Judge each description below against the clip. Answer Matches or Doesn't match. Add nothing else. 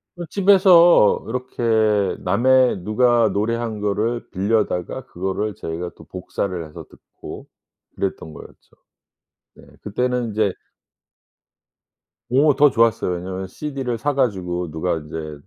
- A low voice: Matches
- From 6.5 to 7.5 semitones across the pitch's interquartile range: Doesn't match